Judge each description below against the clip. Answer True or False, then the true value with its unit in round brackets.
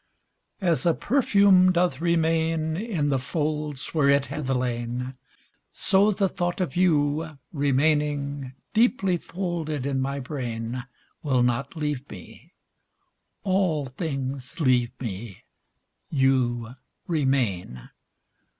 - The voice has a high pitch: False (145 Hz)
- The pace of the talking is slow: True (105 wpm)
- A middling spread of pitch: True (4.7 semitones)